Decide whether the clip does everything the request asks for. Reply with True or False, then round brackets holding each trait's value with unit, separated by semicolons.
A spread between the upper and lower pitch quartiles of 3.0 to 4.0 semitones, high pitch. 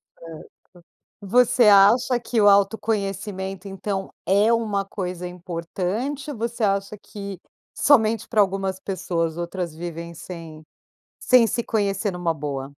True (3.6 semitones; 195 Hz)